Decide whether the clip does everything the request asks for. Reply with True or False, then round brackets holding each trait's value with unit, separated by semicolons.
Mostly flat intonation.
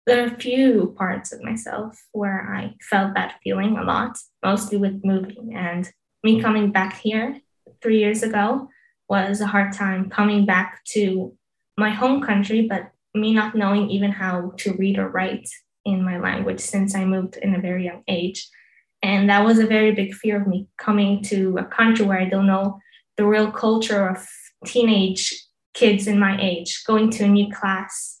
True (2.3 semitones)